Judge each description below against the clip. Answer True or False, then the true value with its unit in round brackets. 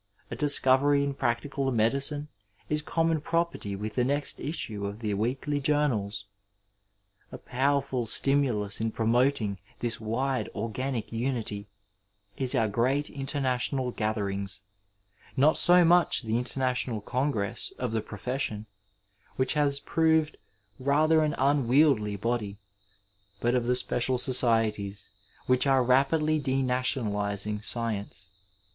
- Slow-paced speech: True (120 wpm)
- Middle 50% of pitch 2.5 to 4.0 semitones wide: False (4.5 semitones)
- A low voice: True (125 Hz)